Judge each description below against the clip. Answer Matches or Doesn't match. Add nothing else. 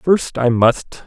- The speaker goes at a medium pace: Matches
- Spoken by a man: Matches